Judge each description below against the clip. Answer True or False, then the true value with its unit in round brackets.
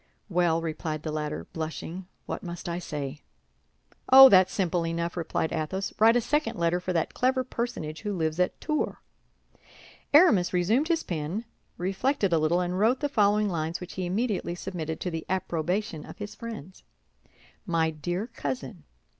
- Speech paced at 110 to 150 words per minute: False (165 wpm)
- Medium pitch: True (180 Hz)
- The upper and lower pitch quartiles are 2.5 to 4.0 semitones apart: False (4.7 semitones)